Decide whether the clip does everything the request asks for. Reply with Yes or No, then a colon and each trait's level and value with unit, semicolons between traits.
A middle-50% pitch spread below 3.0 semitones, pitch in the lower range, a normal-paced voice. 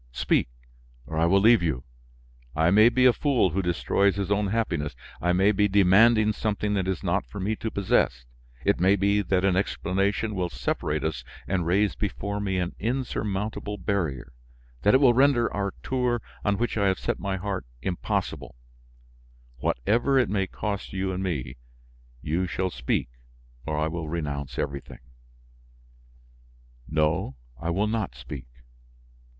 No: average, 3.7 semitones; very low, 95 Hz; average, 160 wpm